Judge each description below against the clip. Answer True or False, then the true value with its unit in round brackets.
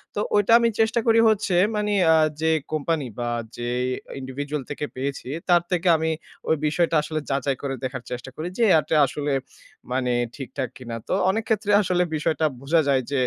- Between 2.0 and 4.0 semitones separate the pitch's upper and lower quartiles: False (4.9 semitones)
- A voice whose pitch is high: False (150 Hz)